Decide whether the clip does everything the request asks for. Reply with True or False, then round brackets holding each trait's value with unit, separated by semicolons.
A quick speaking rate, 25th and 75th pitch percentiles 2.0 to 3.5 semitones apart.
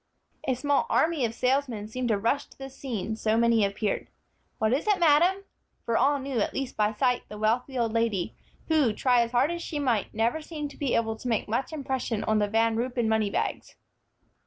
False (210 wpm; 3.9 semitones)